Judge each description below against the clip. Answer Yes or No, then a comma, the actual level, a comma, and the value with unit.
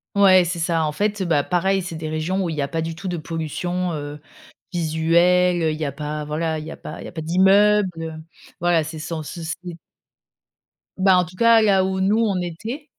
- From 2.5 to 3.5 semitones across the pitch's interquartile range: Yes, average, 2.9 semitones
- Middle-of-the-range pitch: Yes, medium, 175 Hz